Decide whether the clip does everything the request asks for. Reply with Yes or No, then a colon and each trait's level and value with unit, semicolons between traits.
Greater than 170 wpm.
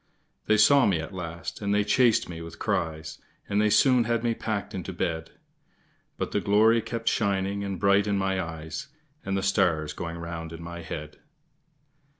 Yes: average, 180 wpm